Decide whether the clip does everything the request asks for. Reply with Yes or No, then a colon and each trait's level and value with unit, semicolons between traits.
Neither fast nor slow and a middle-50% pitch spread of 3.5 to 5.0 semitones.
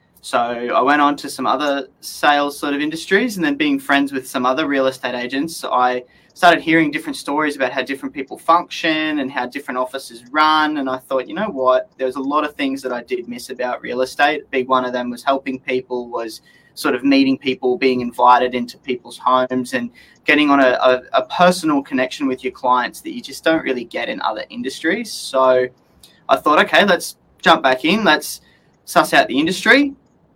No: fast, 210 wpm; average, 3.9 semitones